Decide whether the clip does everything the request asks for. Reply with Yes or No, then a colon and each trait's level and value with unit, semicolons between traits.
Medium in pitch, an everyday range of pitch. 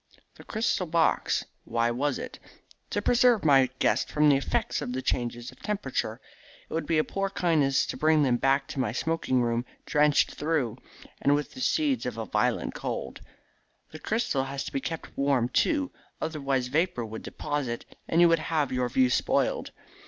Yes: medium, 145 Hz; average, 4.5 semitones